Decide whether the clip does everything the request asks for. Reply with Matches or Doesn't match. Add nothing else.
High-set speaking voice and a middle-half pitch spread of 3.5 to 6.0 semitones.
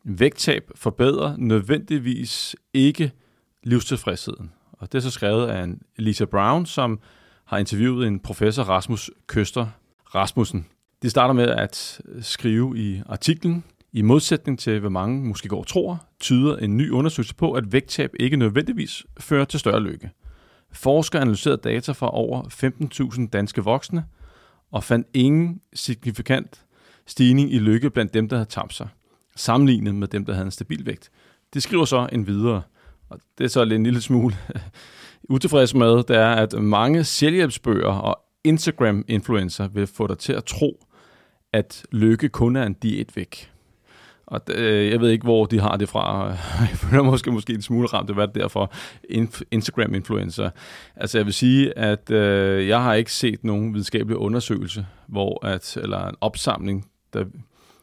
Doesn't match